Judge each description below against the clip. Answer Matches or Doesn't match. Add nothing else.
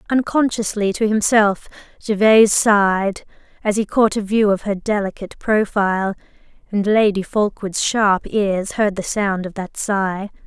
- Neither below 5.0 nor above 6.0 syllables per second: Doesn't match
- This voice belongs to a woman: Matches